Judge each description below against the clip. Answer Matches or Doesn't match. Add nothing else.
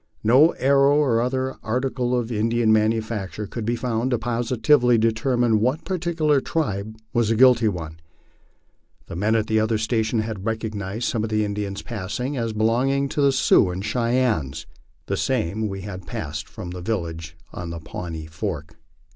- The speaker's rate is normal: Matches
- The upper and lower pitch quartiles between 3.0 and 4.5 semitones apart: Matches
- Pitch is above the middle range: Doesn't match